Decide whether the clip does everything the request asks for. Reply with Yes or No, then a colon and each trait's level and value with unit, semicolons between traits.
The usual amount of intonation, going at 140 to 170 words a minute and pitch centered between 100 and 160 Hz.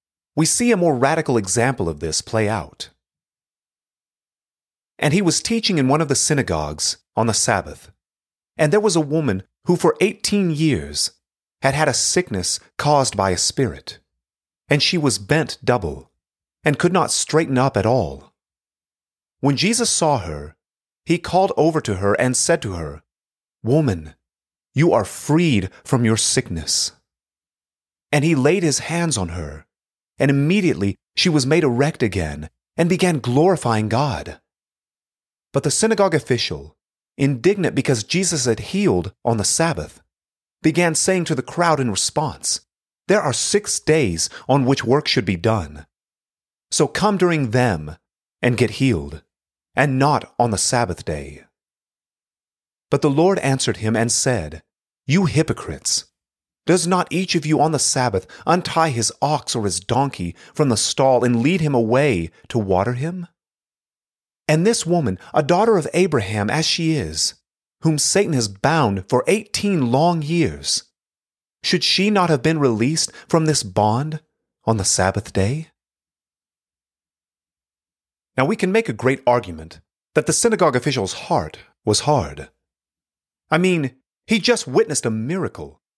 No: wide, 8.7 semitones; average, 150 wpm; low, 135 Hz